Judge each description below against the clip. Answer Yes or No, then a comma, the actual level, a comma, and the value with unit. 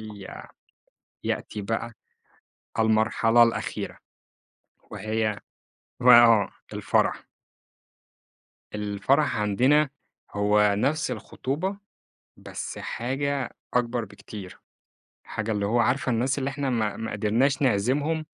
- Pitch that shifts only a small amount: No, average, 4.1 semitones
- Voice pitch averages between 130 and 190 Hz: No, low, 115 Hz